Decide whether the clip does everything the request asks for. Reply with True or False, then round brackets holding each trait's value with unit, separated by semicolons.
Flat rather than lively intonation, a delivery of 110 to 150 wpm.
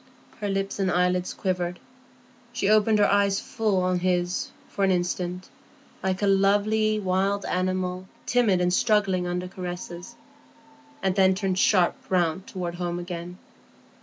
True (1.9 semitones; 140 wpm)